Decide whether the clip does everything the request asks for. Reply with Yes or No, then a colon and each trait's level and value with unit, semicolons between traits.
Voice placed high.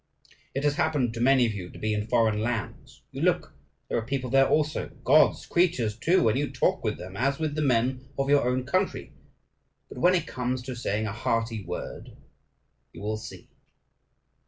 No: low, 125 Hz